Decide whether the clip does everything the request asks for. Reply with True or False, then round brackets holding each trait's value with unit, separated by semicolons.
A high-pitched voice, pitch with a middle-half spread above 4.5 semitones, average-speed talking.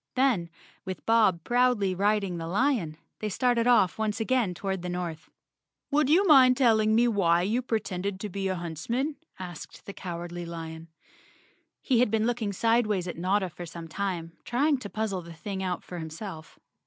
True (200 Hz; 5.0 semitones; 175 wpm)